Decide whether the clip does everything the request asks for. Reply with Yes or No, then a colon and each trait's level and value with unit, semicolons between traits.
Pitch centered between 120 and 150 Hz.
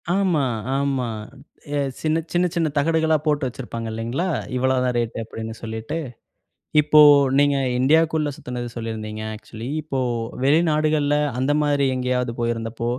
Yes: low, 135 Hz